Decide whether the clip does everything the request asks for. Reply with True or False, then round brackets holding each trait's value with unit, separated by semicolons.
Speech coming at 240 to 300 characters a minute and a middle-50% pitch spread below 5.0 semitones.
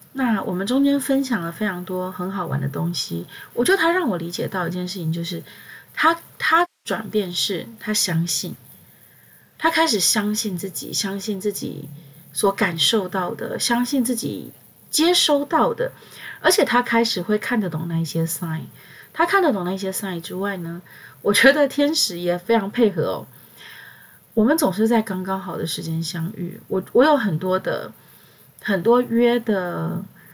False (250 characters per minute; 5.5 semitones)